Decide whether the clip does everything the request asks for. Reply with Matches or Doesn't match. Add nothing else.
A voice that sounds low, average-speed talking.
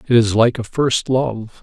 Doesn't match